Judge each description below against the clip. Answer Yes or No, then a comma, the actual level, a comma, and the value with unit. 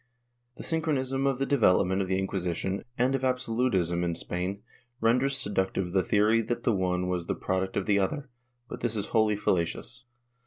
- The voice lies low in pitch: Yes, low, 105 Hz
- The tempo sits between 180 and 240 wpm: Yes, average, 185 wpm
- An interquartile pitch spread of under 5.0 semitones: No, average, 5.3 semitones